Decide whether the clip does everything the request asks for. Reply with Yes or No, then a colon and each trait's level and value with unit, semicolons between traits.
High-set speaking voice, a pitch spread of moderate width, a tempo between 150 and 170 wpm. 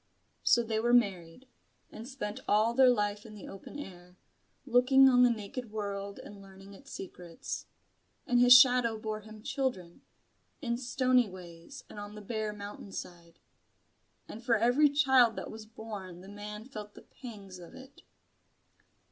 Yes: high, 215 Hz; average, 3.8 semitones; average, 160 wpm